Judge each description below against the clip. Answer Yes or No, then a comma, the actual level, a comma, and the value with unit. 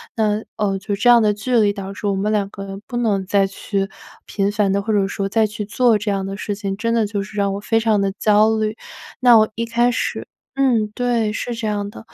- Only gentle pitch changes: Yes, narrow, 2.2 semitones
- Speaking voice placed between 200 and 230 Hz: Yes, high, 210 Hz